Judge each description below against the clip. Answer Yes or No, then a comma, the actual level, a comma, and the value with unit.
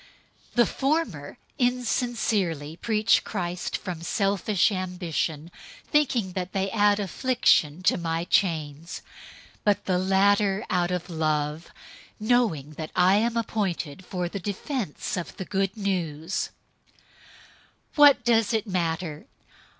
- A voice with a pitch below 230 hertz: Yes, high, 190 Hz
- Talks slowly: Yes, slow, 125 wpm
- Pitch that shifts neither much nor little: Yes, average, 4.2 semitones